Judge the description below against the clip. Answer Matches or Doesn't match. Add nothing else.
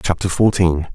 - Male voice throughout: Matches